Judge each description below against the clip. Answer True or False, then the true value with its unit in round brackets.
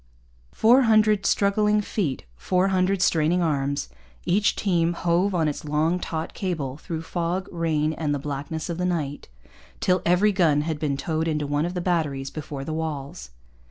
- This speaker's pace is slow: False (170 wpm)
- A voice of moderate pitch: True (165 Hz)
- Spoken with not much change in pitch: False (3.6 semitones)